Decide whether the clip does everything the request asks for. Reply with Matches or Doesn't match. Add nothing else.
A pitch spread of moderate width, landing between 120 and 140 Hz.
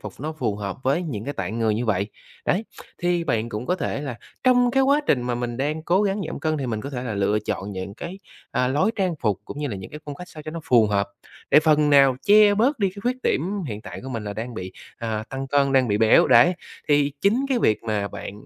Doesn't match